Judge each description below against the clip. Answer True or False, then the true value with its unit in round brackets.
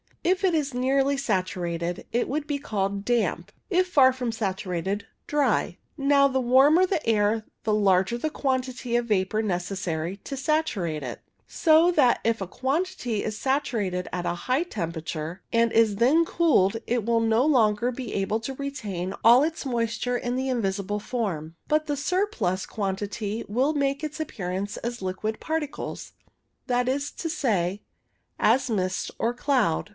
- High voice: True (235 Hz)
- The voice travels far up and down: True (6.0 semitones)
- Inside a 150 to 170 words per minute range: True (160 wpm)